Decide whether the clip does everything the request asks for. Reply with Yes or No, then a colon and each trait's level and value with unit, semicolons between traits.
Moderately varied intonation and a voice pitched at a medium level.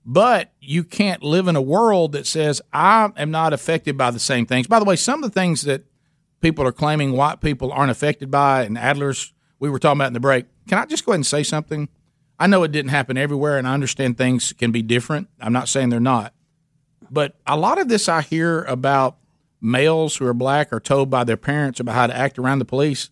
Yes: average, 3.5 semitones; medium, 145 Hz